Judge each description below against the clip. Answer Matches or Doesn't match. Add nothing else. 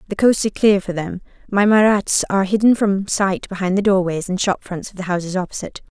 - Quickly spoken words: Matches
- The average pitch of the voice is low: Doesn't match